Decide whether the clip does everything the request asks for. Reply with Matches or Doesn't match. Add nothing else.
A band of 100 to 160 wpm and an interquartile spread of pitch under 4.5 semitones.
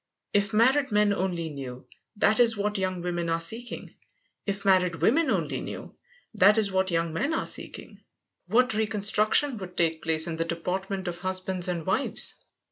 Doesn't match